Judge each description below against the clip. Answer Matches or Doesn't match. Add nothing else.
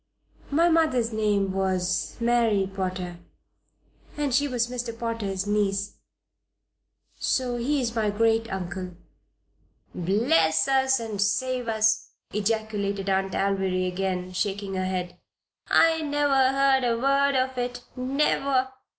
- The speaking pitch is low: Doesn't match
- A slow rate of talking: Matches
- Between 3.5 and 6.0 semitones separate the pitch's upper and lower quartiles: Matches